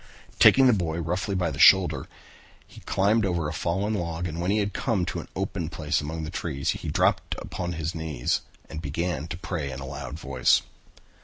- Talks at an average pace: No, fast, 210 wpm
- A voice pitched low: Yes, very low, 85 Hz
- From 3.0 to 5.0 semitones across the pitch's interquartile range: Yes, average, 3.5 semitones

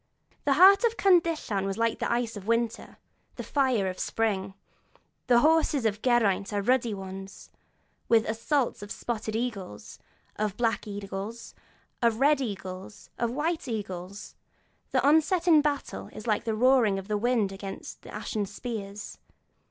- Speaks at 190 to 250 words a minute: No, average, 160 wpm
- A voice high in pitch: Yes, high, 225 Hz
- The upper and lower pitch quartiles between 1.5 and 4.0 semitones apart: No, average, 4.5 semitones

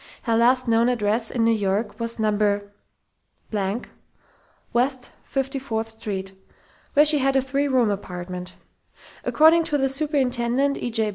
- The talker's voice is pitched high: Yes, high, 235 Hz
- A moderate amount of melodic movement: Yes, average, 3.9 semitones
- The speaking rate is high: No, slow, 135 wpm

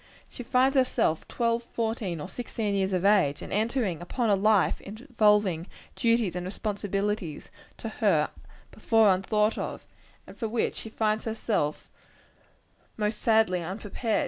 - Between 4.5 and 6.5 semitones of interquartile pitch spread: No, average, 3.2 semitones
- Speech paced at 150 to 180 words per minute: No, average, 140 wpm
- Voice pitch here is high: Yes, high, 210 Hz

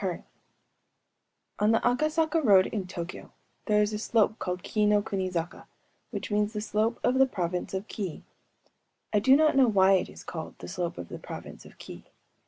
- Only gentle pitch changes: No, average, 3.6 semitones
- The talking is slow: No, average, 190 wpm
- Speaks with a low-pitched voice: No, high, 210 Hz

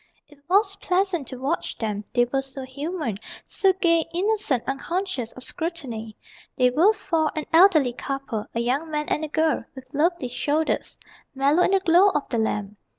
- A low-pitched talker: No, very high, 295 Hz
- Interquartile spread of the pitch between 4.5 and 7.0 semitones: Yes, wide, 5.4 semitones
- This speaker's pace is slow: No, average, 175 wpm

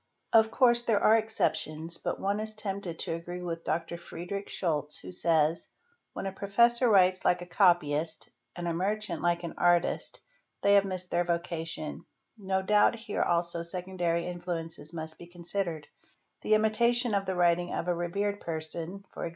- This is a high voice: No, medium, 175 Hz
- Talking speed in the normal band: Yes, average, 175 wpm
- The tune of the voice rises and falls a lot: No, average, 3.1 semitones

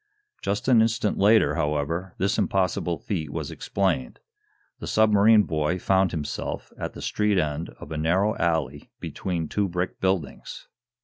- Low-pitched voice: Yes, very low, 95 Hz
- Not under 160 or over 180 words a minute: No, average, 145 wpm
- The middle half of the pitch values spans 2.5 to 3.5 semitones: No, average, 4.1 semitones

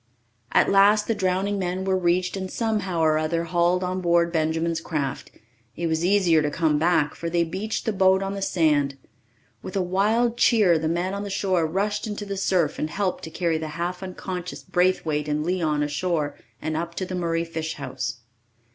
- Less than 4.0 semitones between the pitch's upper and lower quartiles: Yes, average, 3.0 semitones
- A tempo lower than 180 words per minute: No, average, 195 wpm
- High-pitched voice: No, medium, 175 Hz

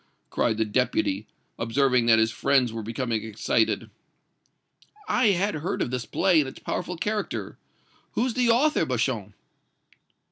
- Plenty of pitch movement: Yes, wide, 8.3 semitones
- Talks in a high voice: No, low, 130 Hz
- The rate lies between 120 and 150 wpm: Yes, average, 140 wpm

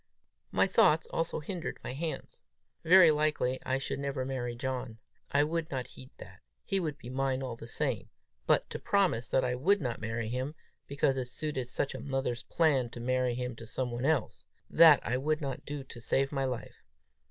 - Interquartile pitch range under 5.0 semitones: Yes, average, 3.3 semitones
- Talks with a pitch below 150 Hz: Yes, low, 135 Hz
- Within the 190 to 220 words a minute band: Yes, average, 200 wpm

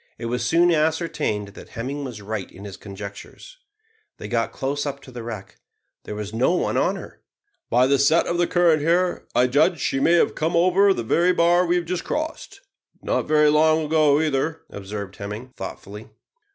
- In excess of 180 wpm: Yes, average, 195 wpm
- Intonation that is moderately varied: No, wide, 7.0 semitones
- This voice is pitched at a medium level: Yes, medium, 145 Hz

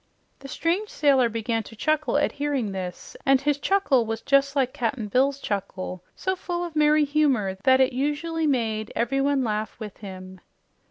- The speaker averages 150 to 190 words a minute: Yes, average, 170 wpm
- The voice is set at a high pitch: Yes, very high, 265 Hz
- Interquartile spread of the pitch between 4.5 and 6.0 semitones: Yes, average, 5.2 semitones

